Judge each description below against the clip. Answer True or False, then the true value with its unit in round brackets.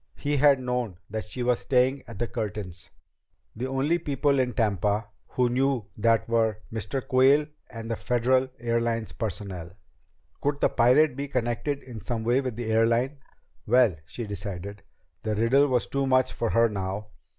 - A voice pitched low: True (120 Hz)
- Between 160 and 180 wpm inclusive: True (165 wpm)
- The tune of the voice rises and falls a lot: False (3.3 semitones)